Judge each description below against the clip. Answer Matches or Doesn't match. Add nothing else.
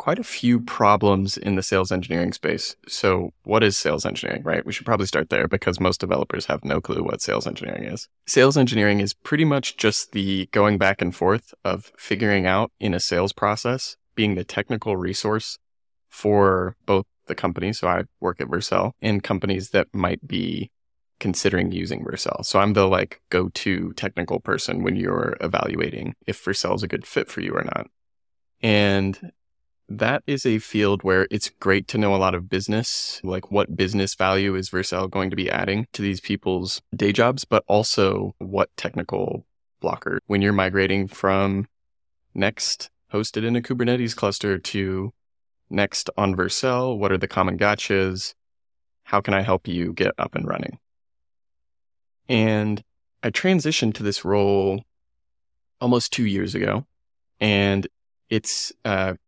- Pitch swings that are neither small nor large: Doesn't match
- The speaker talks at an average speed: Matches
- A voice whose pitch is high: Doesn't match